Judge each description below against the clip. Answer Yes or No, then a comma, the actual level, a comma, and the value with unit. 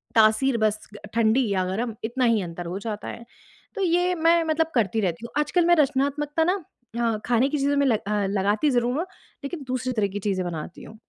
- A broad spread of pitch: Yes, wide, 5.9 semitones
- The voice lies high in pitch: Yes, high, 240 Hz